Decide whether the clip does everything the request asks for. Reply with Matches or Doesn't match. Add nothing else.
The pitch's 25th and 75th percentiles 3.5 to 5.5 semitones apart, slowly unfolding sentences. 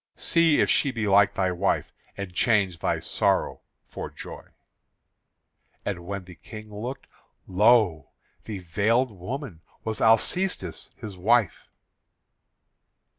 Matches